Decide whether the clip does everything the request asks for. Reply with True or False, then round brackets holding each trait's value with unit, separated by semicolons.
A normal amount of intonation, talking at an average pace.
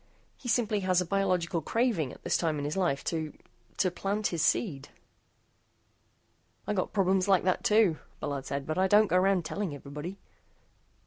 True (4.0 semitones; 175 wpm)